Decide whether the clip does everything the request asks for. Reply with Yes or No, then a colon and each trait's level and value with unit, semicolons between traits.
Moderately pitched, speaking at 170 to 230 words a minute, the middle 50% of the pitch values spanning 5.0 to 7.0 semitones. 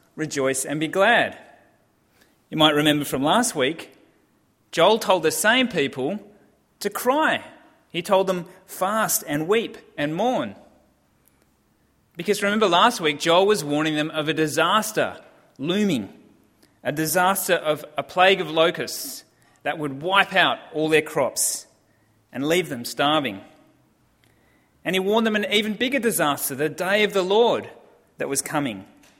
No: medium, 175 Hz; average, 145 wpm; wide, 5.4 semitones